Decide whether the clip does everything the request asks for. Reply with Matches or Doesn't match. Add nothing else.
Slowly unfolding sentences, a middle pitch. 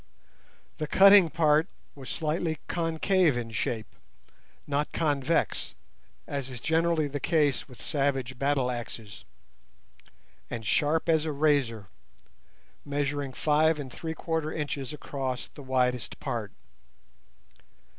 Matches